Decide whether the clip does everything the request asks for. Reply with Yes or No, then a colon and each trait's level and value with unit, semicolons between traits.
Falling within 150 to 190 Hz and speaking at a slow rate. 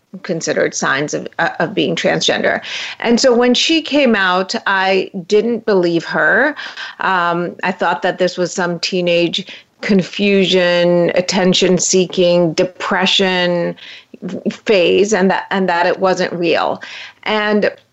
Yes: medium, 185 Hz; slow, 125 wpm